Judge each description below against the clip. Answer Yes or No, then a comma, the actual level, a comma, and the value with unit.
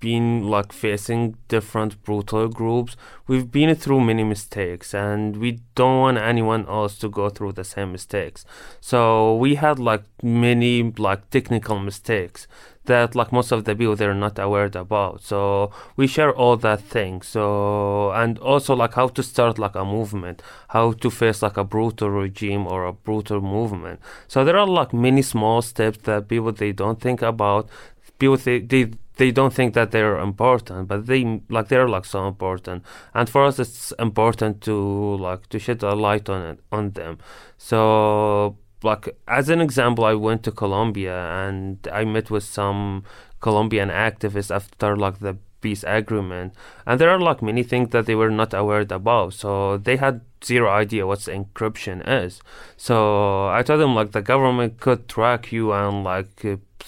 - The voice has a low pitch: Yes, low, 110 Hz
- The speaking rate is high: No, average, 175 wpm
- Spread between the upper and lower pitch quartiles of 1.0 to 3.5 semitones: Yes, average, 2.9 semitones